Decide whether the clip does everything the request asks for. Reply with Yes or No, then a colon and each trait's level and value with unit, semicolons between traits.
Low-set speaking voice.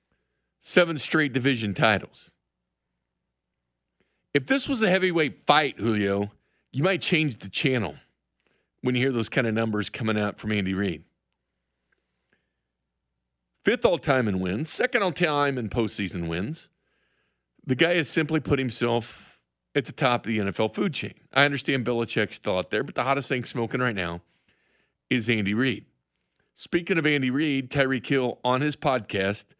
Yes: low, 120 Hz